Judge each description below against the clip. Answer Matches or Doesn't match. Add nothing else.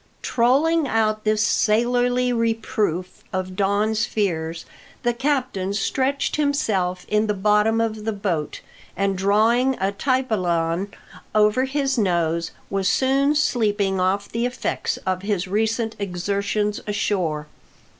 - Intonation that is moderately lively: Matches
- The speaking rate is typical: Doesn't match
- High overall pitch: Matches